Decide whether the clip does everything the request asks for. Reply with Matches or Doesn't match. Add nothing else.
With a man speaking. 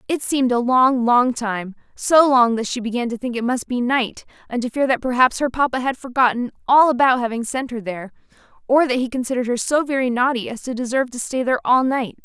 Doesn't match